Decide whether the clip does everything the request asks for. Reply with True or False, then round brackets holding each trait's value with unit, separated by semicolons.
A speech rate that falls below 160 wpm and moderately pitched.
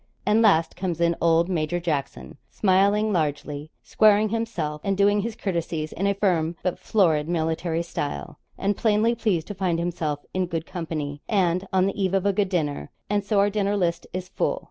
False (190 wpm; 180 Hz)